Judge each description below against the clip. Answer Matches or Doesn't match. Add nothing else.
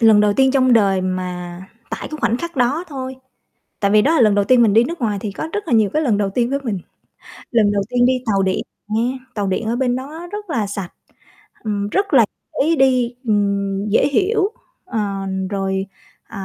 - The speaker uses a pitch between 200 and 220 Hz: Doesn't match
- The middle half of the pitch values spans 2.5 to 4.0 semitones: Doesn't match